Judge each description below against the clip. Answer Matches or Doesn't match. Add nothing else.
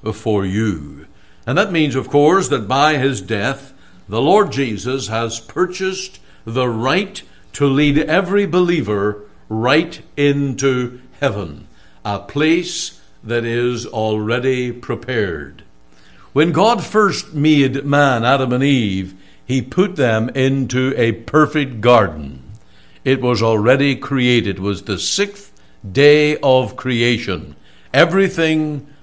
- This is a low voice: Matches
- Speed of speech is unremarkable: Doesn't match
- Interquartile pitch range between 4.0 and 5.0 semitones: Doesn't match